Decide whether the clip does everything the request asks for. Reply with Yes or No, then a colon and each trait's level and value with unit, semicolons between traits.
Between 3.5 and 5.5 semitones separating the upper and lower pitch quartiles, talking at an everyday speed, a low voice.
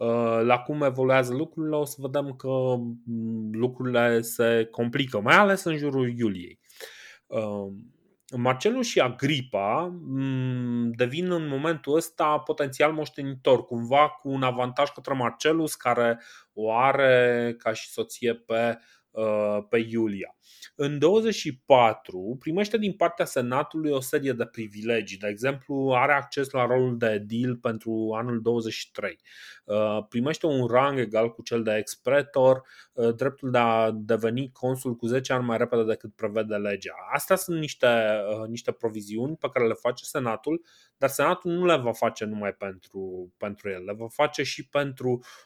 Yes: average, 3.9 semitones; average, 140 wpm; low, 125 Hz